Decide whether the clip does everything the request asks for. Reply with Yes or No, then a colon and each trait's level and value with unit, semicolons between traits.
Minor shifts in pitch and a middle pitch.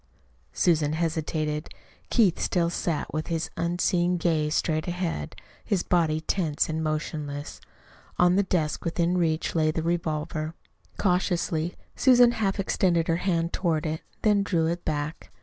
Yes: narrow, 2.3 semitones; medium, 165 Hz